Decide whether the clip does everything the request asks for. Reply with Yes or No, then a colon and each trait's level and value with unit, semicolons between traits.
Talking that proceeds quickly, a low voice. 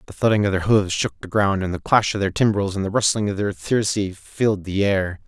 Yes: fast, 260 wpm; low, 100 Hz